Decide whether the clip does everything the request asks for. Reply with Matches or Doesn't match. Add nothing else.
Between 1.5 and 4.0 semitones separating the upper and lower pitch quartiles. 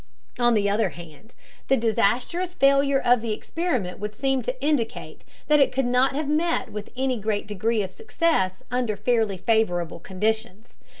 Doesn't match